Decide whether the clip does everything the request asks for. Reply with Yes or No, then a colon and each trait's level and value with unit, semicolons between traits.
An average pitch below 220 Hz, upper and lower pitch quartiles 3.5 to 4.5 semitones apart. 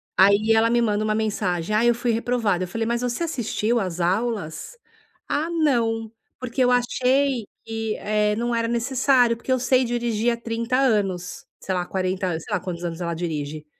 No: high, 225 Hz; average, 4.0 semitones